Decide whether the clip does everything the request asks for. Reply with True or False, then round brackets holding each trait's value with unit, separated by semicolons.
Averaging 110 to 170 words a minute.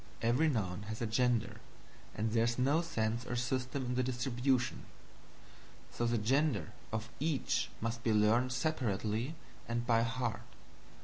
True (145 wpm)